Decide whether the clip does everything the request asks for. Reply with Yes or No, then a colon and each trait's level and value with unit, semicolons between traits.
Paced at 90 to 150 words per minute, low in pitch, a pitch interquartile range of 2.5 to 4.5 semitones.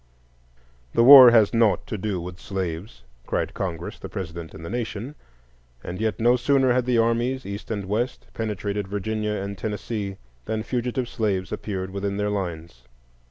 No: average, 160 wpm; low, 105 Hz; average, 3.5 semitones